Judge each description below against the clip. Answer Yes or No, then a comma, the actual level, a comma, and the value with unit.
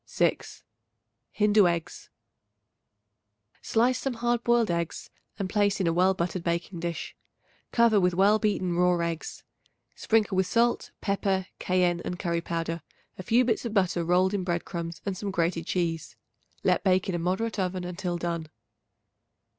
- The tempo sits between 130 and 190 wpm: Yes, average, 155 wpm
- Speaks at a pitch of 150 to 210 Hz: Yes, medium, 185 Hz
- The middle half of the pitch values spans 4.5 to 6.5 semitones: No, average, 3.3 semitones